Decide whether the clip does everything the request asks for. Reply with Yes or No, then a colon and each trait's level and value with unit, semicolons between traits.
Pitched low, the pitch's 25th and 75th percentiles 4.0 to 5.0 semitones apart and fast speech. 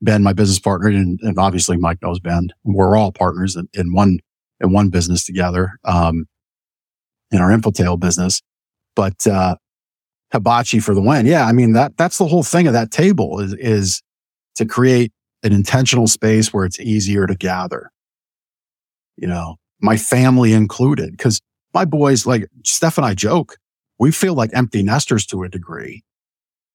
No: low, 100 Hz; average, 4.4 semitones; average, 170 wpm